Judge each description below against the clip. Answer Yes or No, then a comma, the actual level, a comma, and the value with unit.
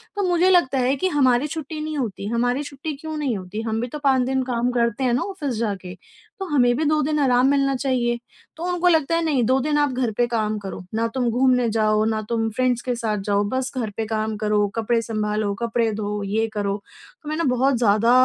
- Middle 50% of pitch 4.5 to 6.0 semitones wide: No, average, 4.1 semitones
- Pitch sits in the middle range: No, high, 245 Hz